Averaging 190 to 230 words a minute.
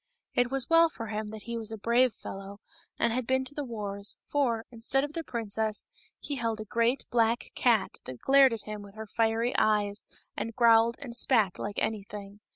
Yes: average, 200 wpm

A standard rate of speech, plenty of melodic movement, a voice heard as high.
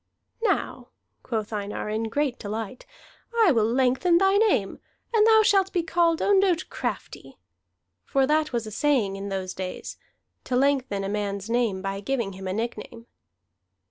Yes: average, 155 wpm; wide, 8.3 semitones; high, 240 Hz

